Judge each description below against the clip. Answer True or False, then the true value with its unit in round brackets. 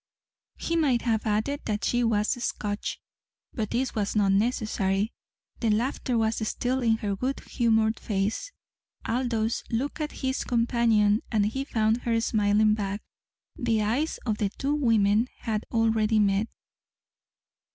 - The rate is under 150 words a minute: True (140 wpm)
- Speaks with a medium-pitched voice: False (225 Hz)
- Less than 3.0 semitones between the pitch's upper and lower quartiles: True (2.5 semitones)